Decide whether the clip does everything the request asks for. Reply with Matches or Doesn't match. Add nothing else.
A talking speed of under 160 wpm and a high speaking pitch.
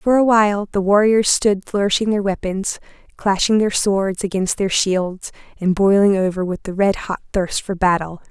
Doesn't match